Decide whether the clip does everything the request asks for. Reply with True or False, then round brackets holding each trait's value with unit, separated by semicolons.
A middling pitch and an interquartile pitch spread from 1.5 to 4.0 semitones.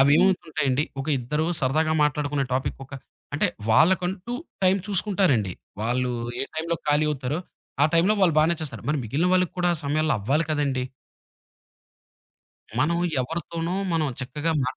True (155 Hz; 3.7 semitones)